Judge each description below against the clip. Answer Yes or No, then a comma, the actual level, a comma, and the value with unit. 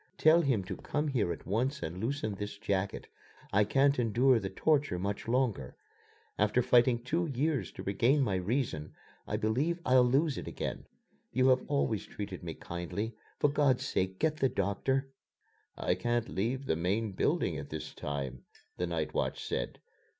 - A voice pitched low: Yes, low, 115 Hz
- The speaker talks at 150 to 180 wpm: Yes, average, 170 wpm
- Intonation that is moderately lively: No, wide, 6.1 semitones